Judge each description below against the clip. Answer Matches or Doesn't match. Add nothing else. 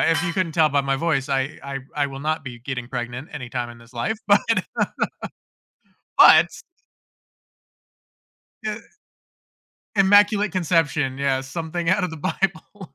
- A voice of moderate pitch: Matches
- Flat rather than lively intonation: Doesn't match